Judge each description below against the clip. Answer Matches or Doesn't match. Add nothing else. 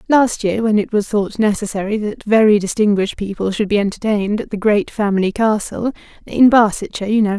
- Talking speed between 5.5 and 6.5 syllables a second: Matches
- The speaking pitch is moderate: Doesn't match